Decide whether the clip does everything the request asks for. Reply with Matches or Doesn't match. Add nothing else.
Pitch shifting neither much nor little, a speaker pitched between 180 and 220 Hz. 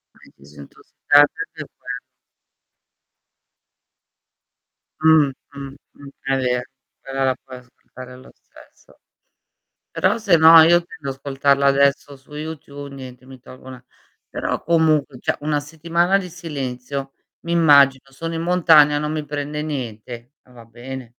Doesn't match